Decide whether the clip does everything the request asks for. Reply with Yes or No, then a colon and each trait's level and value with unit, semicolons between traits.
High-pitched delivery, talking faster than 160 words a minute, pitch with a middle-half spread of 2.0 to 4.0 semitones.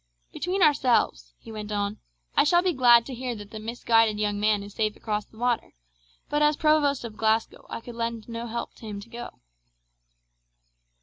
Yes: high, 230 Hz; average, 185 wpm; average, 2.8 semitones